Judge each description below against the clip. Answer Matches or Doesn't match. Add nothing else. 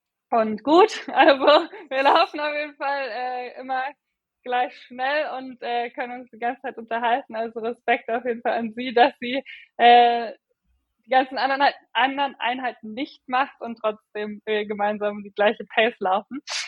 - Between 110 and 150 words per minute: Doesn't match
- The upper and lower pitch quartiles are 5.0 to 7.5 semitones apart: Doesn't match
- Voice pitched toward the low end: Doesn't match